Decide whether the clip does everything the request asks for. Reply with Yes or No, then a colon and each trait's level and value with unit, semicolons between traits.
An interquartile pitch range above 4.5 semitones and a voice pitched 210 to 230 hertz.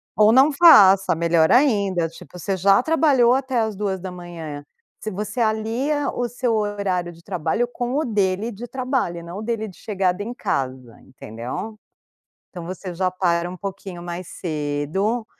No: average, 5.1 semitones; high, 195 Hz